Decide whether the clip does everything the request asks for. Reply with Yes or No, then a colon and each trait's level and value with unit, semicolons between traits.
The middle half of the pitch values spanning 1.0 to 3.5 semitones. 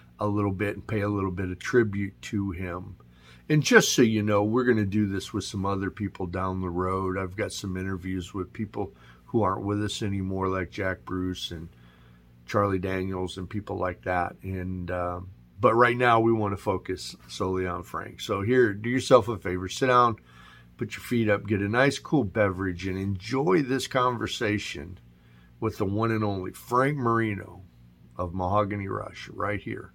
Yes: average, 2.9 semitones